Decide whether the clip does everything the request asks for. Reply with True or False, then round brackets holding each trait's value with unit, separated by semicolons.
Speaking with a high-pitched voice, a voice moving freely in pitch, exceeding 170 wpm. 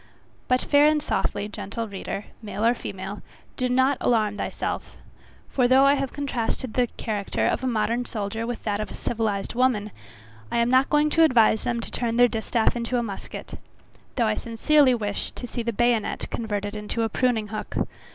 False (235 Hz; 3.0 semitones; 190 wpm)